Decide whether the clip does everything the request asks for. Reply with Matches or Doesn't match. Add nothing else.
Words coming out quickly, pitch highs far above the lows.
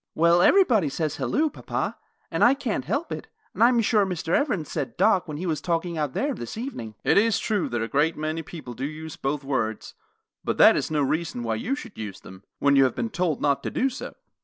Matches